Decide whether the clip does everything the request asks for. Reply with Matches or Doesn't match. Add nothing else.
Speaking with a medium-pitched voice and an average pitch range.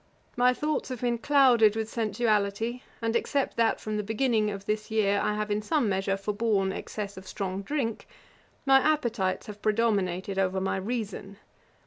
Doesn't match